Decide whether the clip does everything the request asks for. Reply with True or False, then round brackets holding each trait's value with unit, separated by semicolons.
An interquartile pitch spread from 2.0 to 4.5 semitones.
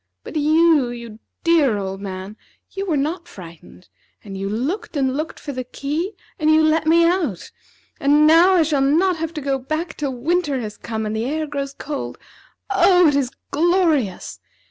False (5.2 semitones)